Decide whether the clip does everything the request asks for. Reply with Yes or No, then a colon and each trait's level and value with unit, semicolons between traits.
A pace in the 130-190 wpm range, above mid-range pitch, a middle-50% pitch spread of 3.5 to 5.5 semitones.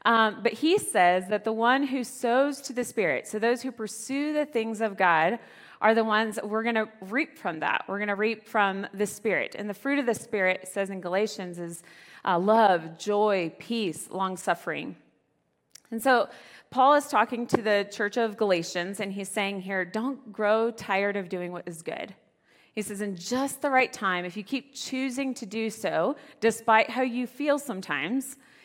No: average, 200 wpm; high, 220 Hz; average, 4.2 semitones